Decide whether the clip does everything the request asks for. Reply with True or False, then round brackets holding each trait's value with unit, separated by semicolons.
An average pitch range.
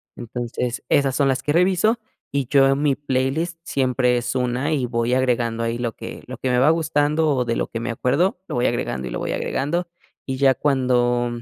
True (3.2 semitones)